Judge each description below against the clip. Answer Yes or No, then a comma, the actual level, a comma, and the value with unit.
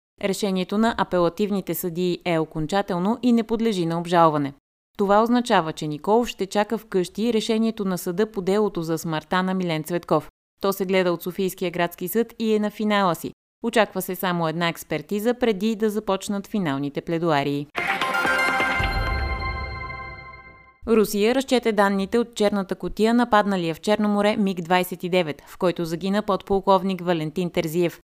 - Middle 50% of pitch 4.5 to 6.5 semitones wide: No, average, 3.8 semitones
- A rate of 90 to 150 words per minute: Yes, average, 145 wpm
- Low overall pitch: No, medium, 185 Hz